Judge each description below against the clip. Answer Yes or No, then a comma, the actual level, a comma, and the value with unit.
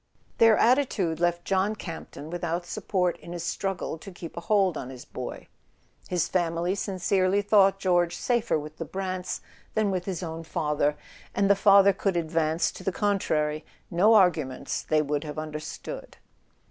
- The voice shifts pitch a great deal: No, average, 3.5 semitones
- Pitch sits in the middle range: Yes, medium, 180 Hz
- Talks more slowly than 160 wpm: No, average, 170 wpm